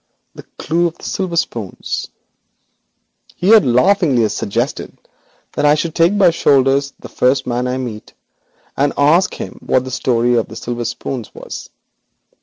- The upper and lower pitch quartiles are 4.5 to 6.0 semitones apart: Yes, wide, 5.6 semitones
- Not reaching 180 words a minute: Yes, average, 160 wpm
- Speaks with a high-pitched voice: No, low, 135 Hz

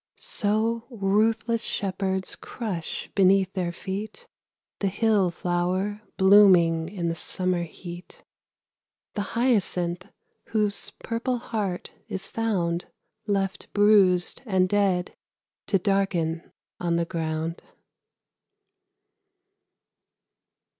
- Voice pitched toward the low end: No, high, 195 Hz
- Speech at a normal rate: No, slow, 90 wpm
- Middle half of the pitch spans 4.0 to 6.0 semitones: No, average, 3.0 semitones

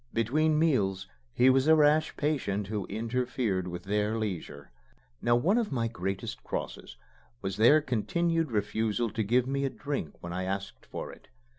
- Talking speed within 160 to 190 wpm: Yes, average, 165 wpm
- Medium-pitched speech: No, low, 115 Hz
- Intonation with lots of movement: Yes, wide, 6.1 semitones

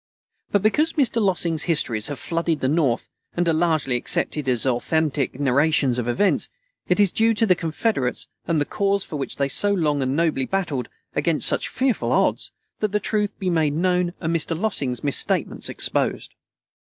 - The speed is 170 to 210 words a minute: Yes, average, 180 wpm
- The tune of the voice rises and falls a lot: Yes, wide, 5.7 semitones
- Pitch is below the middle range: No, medium, 165 Hz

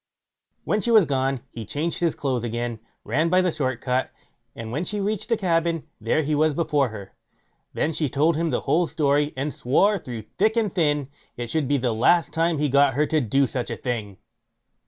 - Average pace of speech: No, fast, 210 wpm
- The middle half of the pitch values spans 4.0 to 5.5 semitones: Yes, average, 4.9 semitones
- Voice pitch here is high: No, medium, 145 Hz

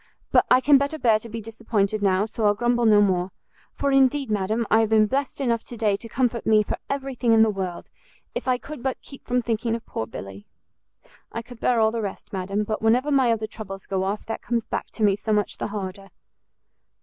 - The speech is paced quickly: Yes, fast, 235 wpm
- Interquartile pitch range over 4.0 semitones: No, average, 2.9 semitones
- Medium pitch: No, high, 225 Hz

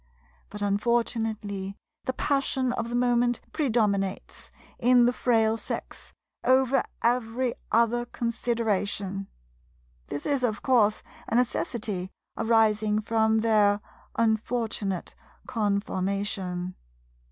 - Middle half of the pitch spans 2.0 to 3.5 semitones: Yes, average, 2.9 semitones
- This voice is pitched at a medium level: No, high, 225 Hz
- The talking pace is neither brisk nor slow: No, slow, 95 wpm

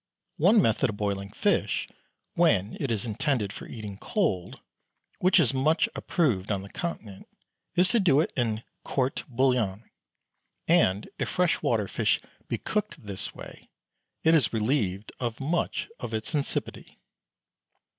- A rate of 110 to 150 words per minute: Yes, average, 145 wpm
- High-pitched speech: No, low, 120 Hz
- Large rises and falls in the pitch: Yes, wide, 7.6 semitones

